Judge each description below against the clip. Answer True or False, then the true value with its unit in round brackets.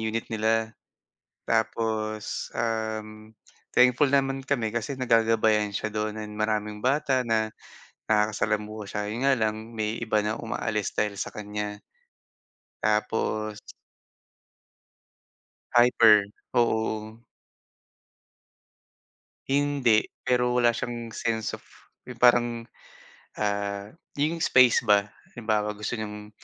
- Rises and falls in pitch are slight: True (1.9 semitones)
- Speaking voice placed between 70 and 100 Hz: False (110 Hz)